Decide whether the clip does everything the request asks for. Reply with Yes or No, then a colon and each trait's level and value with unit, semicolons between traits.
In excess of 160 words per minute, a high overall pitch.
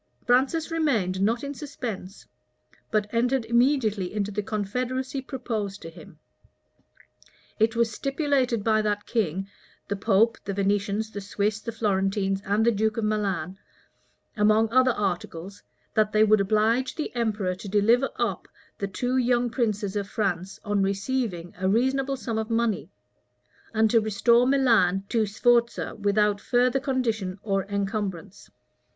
No: average, 145 wpm; high, 215 Hz